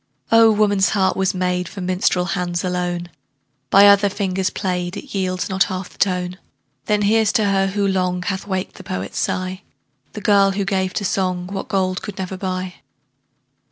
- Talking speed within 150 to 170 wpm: No, average, 180 wpm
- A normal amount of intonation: No, narrow, 1.6 semitones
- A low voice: No, high, 190 Hz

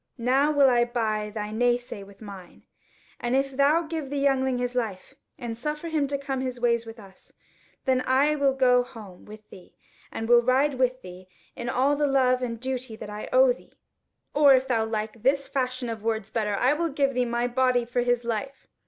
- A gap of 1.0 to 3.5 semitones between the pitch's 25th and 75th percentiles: Yes, average, 3.2 semitones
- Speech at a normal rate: No, fast, 210 wpm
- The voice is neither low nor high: No, very high, 250 Hz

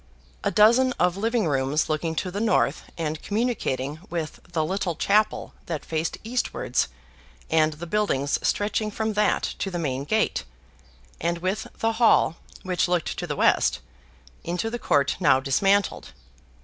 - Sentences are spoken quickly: No, average, 150 wpm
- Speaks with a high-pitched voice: No, medium, 175 Hz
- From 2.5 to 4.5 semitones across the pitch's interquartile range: No, wide, 5.4 semitones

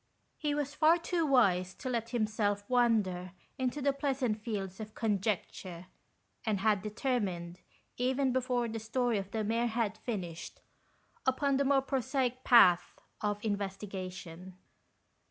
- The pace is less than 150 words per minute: Yes, slow, 135 wpm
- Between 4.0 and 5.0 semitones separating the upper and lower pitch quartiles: Yes, average, 4.7 semitones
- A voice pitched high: Yes, high, 225 Hz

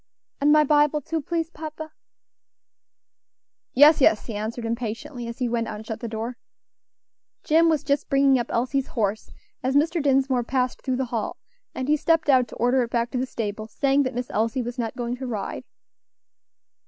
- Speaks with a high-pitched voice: Yes, very high, 255 Hz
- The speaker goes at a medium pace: Yes, average, 190 wpm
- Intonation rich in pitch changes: No, average, 3.6 semitones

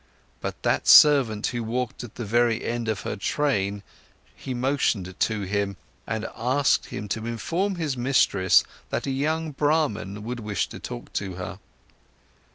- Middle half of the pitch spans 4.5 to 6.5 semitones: Yes, average, 5.1 semitones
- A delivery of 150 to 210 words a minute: Yes, average, 160 wpm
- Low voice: Yes, low, 115 Hz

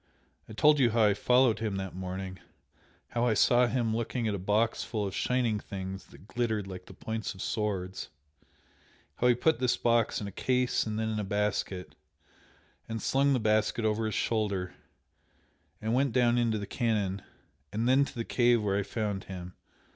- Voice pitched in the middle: No, low, 110 Hz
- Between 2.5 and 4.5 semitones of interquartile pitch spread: Yes, average, 3.1 semitones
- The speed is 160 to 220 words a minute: Yes, average, 190 wpm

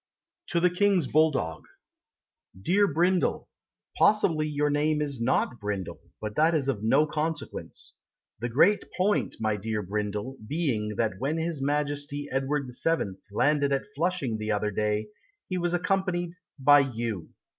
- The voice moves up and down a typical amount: No, wide, 6.9 semitones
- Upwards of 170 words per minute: No, average, 145 wpm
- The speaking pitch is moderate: Yes, medium, 145 Hz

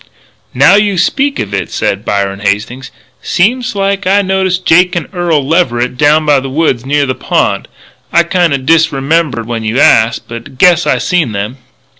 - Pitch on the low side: No, medium, 150 Hz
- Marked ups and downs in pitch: Yes, wide, 6.9 semitones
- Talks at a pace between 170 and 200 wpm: Yes, average, 175 wpm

